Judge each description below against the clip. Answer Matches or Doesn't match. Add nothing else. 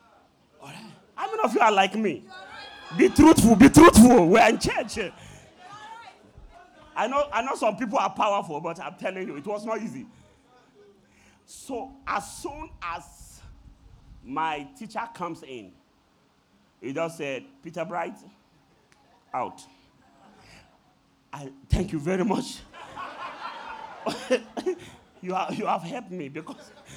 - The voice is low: Doesn't match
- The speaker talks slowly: Matches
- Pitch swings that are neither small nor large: Doesn't match